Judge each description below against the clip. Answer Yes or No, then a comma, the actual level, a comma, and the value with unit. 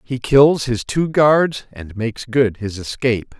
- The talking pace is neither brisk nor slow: Yes, average, 175 wpm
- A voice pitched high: No, low, 125 Hz